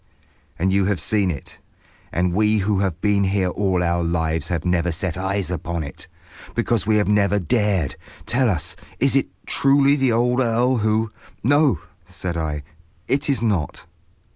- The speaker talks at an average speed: Yes, average, 165 wpm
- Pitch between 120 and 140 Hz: No, low, 100 Hz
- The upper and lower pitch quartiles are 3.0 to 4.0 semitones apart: No, average, 4.6 semitones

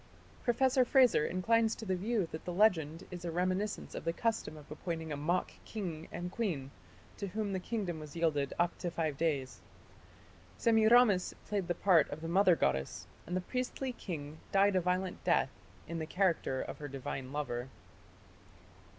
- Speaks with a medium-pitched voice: Yes, medium, 180 Hz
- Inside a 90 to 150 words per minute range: No, average, 175 wpm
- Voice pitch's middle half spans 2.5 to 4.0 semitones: No, average, 4.7 semitones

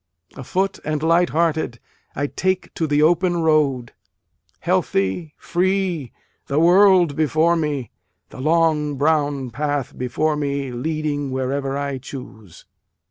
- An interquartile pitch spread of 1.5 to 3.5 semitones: Yes, average, 3.2 semitones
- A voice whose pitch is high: No, medium, 150 Hz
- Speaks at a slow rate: Yes, slow, 120 wpm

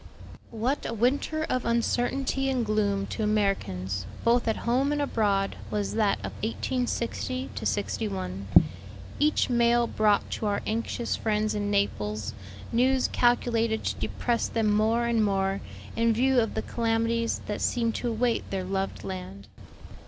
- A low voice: No, high, 225 Hz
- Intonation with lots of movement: No, average, 3.0 semitones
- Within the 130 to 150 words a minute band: Yes, average, 145 wpm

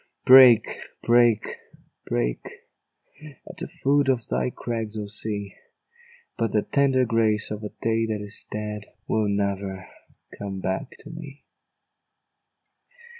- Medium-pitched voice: No, low, 110 Hz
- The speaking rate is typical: No, slow, 125 wpm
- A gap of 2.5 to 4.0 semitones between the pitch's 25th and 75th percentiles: Yes, average, 3.1 semitones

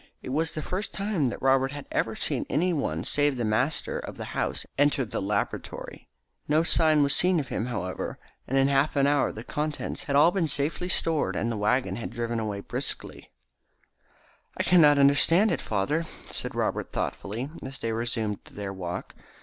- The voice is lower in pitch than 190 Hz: Yes, medium, 140 Hz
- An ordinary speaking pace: Yes, average, 190 wpm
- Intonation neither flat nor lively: Yes, average, 4.9 semitones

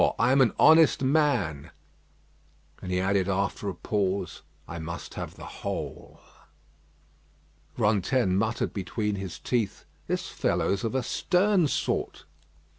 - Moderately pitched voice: No, low, 105 Hz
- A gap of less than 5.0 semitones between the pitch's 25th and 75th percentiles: No, wide, 5.6 semitones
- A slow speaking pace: Yes, slow, 125 wpm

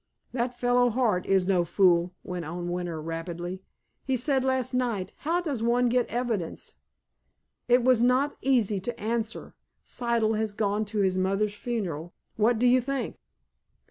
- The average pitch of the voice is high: Yes, high, 220 Hz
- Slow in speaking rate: No, average, 155 wpm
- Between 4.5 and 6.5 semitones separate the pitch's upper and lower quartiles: Yes, average, 4.9 semitones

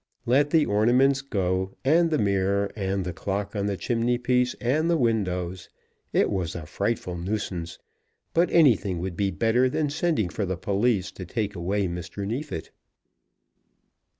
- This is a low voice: Yes, low, 100 Hz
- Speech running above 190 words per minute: No, average, 155 wpm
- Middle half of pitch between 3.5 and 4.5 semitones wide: No, average, 5.0 semitones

